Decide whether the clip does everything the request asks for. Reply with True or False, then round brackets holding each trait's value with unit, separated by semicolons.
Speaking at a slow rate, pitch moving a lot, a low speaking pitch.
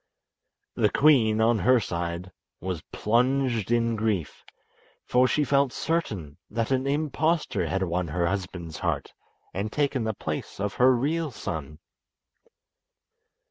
True (130 wpm; 6.6 semitones; 115 Hz)